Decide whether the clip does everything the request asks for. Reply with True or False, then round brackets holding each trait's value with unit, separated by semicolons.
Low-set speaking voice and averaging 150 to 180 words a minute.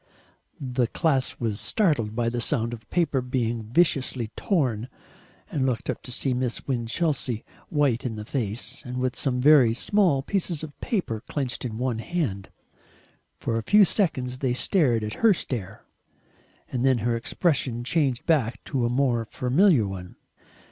True (125 Hz; 160 wpm)